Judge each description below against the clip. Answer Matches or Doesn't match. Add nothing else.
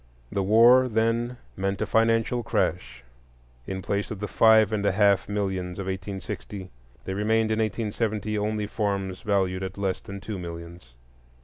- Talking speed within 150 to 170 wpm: Matches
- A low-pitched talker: Matches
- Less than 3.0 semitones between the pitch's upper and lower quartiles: Matches